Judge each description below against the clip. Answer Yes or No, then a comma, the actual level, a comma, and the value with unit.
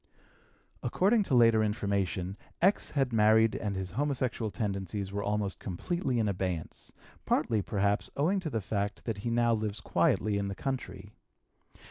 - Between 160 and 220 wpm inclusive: No, average, 150 wpm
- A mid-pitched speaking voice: No, low, 105 Hz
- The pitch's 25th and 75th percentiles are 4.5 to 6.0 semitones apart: No, average, 3.4 semitones